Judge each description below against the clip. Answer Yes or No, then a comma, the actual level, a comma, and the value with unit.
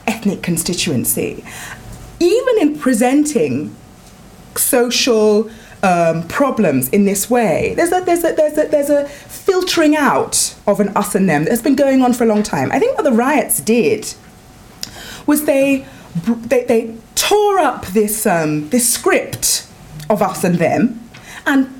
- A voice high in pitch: Yes, high, 240 Hz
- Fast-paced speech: No, average, 150 wpm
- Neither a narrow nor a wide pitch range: No, wide, 6.1 semitones